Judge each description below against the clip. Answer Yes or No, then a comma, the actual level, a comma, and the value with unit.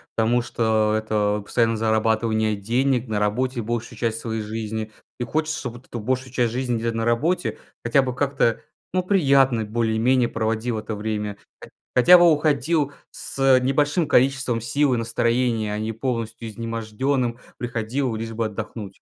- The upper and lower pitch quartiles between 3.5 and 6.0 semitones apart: No, average, 2.9 semitones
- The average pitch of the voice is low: Yes, low, 115 Hz